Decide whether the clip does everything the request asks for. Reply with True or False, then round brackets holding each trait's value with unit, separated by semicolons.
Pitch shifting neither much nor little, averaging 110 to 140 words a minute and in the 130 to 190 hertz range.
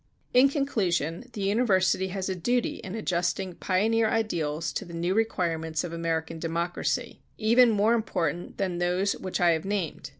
False (4.3 semitones; 160 wpm; 185 Hz)